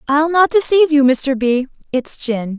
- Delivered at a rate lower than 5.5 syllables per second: Yes, 4.6 syllables/s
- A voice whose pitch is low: No, very high, 280 Hz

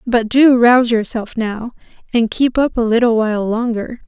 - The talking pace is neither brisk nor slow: Yes, average, 175 wpm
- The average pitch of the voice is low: No, high, 235 Hz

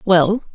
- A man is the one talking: No, female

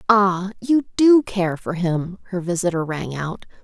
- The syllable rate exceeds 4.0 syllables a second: No, 3.9 syllables/s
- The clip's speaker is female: Yes, female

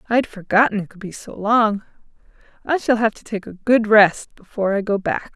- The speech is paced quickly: Yes, fast, 225 wpm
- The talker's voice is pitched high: Yes, high, 210 Hz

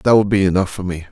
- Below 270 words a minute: No, fast, 320 wpm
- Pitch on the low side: Yes, very low, 95 Hz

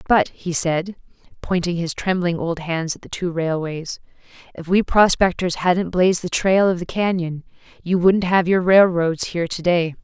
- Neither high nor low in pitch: Yes, medium, 175 Hz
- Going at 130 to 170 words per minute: No, average, 180 wpm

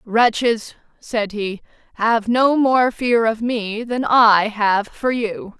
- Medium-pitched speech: No, high, 225 Hz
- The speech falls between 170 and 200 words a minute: No, average, 150 wpm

